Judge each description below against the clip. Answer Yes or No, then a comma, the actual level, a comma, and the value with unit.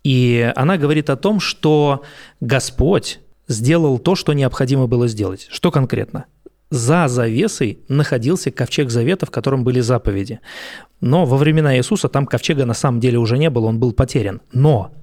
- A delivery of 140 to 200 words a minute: Yes, fast, 160 wpm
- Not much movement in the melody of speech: No, average, 3.7 semitones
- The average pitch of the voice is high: No, low, 135 Hz